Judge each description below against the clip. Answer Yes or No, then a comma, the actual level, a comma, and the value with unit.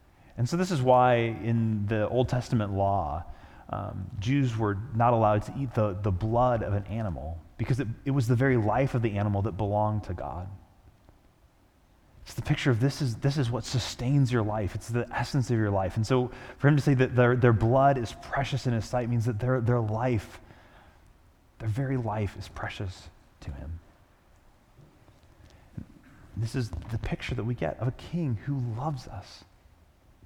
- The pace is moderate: Yes, average, 190 wpm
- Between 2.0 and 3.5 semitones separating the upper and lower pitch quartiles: No, average, 4.2 semitones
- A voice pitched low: Yes, low, 110 Hz